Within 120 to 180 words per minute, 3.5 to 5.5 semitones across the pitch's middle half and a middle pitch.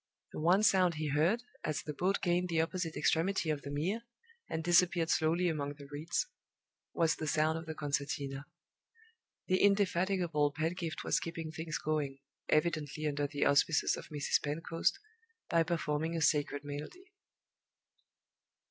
No: average, 150 wpm; average, 2.8 semitones; medium, 160 Hz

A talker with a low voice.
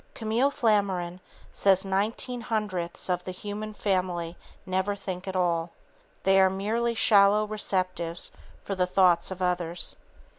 No: high, 190 Hz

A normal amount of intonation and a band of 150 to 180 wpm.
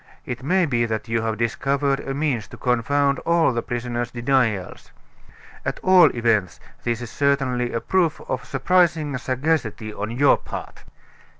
Yes: average, 3.5 semitones; average, 155 wpm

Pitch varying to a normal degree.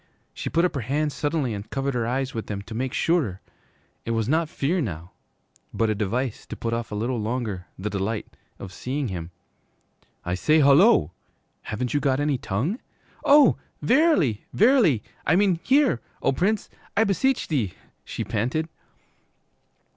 No: wide, 7.0 semitones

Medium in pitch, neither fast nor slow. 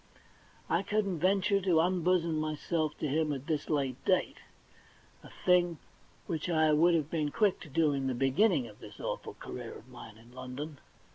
Yes: medium, 155 Hz; average, 180 wpm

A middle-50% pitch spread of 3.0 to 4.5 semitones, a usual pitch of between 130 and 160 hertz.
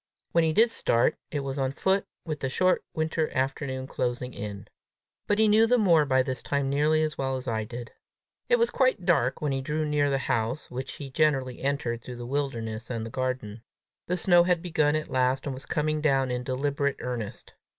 Yes: average, 3.6 semitones; low, 135 Hz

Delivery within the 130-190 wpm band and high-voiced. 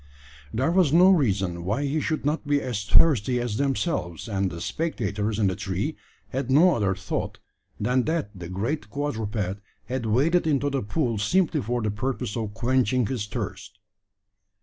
No: average, 170 wpm; low, 120 Hz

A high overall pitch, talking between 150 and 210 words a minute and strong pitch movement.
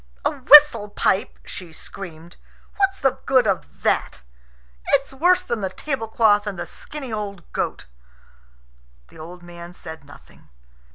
No: high, 205 Hz; slow, 135 wpm; wide, 7.5 semitones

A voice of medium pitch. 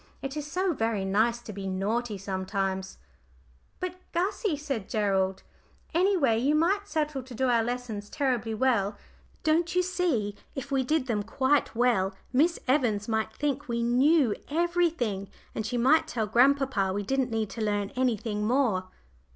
No: high, 245 Hz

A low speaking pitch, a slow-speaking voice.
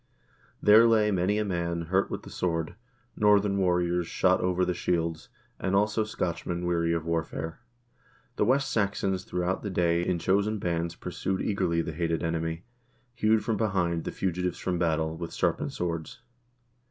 No: very low, 90 Hz; average, 160 wpm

